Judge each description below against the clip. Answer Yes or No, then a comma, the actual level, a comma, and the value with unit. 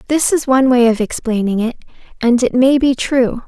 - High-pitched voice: Yes, very high, 250 Hz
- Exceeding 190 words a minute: Yes, fast, 205 wpm